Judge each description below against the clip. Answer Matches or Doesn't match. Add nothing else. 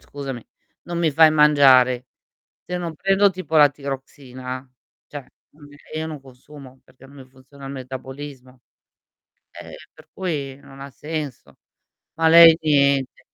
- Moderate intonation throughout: Matches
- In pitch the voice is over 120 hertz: Matches